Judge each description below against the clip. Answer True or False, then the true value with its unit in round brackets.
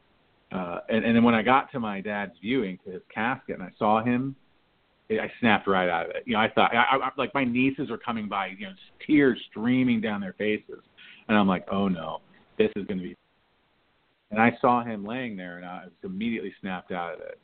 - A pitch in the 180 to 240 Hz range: False (115 Hz)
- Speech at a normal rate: False (235 wpm)